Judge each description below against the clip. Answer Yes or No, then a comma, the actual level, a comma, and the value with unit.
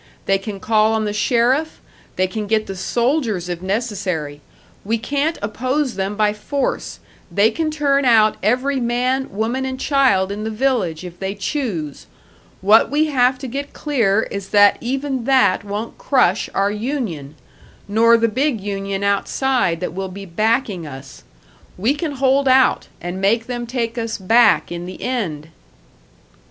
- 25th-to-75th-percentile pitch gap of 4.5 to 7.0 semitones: Yes, average, 4.9 semitones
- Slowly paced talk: No, average, 160 wpm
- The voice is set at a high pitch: Yes, high, 220 Hz